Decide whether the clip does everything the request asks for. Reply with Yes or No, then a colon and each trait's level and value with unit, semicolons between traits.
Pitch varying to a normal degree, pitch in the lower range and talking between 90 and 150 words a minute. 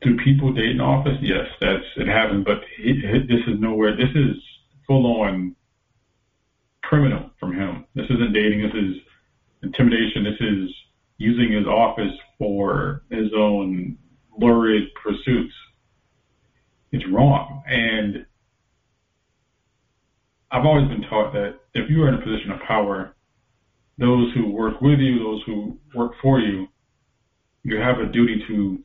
Yes: average, 3.2 semitones; low, 115 Hz; average, 145 wpm